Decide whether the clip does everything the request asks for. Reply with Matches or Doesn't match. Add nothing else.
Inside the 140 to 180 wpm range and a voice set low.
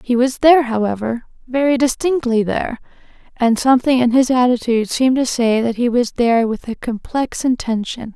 Doesn't match